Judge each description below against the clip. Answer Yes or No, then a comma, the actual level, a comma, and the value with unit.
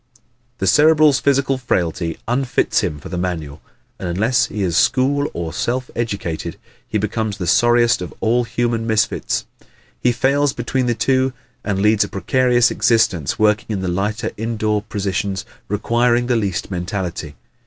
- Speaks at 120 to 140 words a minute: No, average, 155 wpm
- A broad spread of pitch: No, average, 4.3 semitones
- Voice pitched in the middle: No, low, 110 Hz